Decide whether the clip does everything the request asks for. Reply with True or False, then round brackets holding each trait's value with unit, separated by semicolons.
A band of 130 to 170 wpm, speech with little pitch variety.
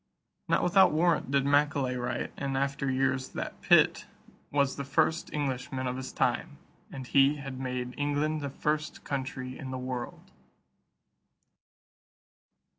True (135 wpm; 1.9 semitones)